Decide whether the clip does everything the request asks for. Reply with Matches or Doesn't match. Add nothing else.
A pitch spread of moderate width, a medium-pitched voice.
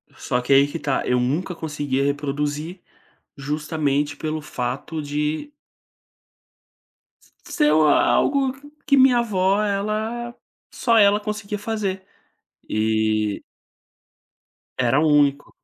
Doesn't match